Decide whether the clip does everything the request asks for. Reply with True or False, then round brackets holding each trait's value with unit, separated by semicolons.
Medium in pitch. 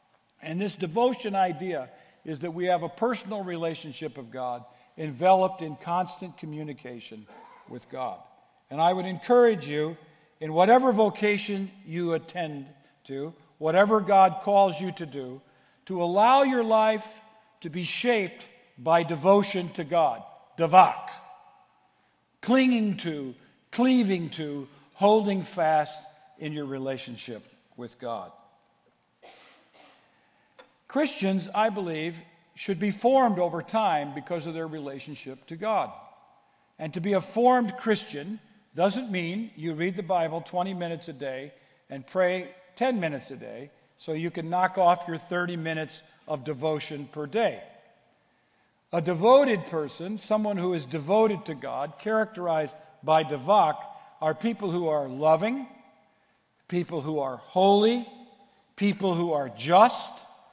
True (175 Hz)